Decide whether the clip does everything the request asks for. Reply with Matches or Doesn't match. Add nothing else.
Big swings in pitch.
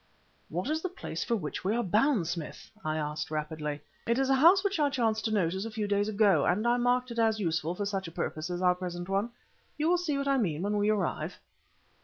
Matches